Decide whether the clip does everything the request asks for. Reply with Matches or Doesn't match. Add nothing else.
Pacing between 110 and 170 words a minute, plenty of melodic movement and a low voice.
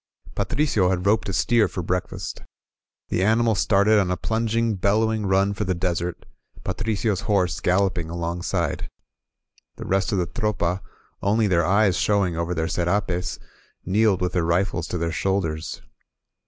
Doesn't match